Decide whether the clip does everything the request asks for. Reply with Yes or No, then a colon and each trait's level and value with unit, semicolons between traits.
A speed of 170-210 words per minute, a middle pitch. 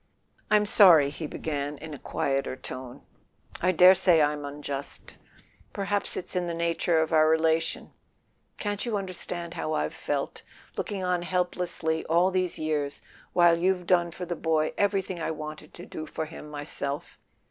No: average, 160 wpm; medium, 165 Hz